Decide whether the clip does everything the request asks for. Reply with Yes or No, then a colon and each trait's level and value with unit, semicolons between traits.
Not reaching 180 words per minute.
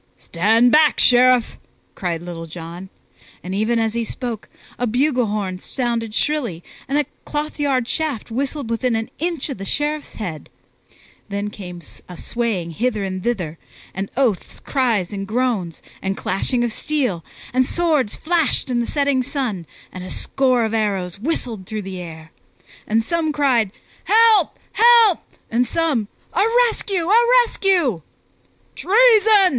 Yes: average, 145 wpm